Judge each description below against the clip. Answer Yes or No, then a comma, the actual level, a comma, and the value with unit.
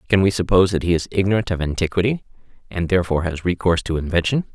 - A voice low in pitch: Yes, very low, 90 Hz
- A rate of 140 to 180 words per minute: No, average, 200 wpm